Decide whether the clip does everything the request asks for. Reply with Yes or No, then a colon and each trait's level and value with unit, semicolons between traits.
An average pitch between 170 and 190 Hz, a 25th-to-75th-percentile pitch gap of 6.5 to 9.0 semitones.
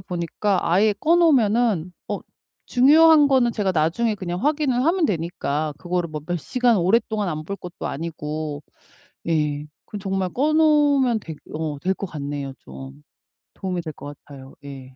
Yes: medium, 185 Hz; wide, 7.8 semitones